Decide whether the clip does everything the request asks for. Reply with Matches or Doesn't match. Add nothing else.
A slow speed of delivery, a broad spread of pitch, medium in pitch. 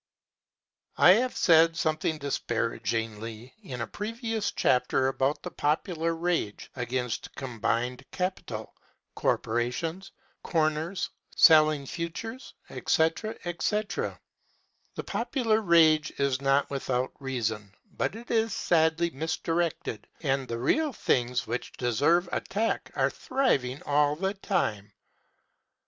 Matches